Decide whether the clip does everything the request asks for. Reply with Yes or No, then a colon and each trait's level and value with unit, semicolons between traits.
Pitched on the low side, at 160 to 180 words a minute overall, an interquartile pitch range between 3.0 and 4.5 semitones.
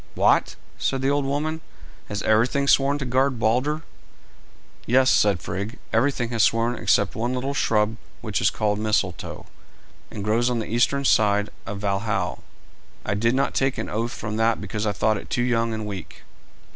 Yes: low, 115 Hz; average, 175 wpm; average, 3.7 semitones